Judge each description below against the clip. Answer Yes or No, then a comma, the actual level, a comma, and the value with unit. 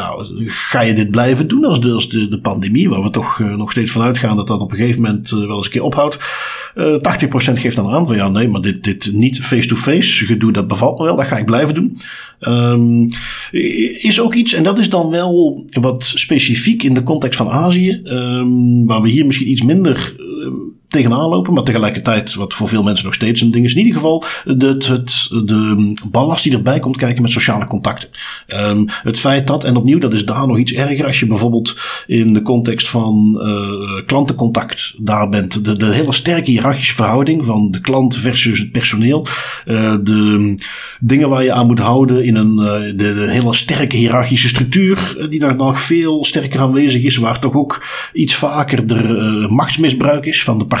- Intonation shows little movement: No, average, 4.2 semitones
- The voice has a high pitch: No, low, 120 Hz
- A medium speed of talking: No, fast, 210 wpm